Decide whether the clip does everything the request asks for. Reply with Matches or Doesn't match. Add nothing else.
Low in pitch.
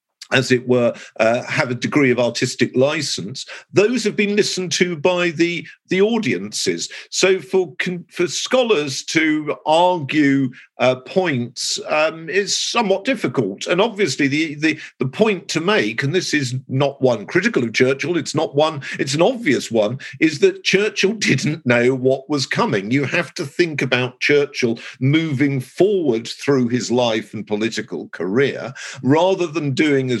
Doesn't match